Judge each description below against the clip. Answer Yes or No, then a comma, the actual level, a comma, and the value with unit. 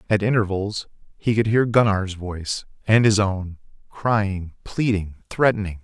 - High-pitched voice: No, low, 100 Hz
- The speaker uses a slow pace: Yes, slow, 115 wpm